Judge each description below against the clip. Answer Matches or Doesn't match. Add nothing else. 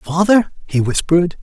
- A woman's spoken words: Doesn't match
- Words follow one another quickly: Doesn't match